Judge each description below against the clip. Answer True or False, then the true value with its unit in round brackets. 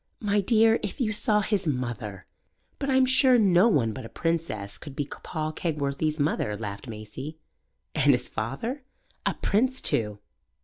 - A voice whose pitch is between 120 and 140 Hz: False (155 Hz)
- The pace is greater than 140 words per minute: True (160 wpm)